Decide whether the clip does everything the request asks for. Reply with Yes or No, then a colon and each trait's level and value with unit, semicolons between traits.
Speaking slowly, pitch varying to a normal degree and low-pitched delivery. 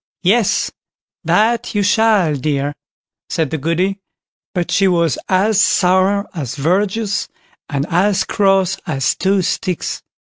No: slow, 120 wpm; average, 3.8 semitones; medium, 185 Hz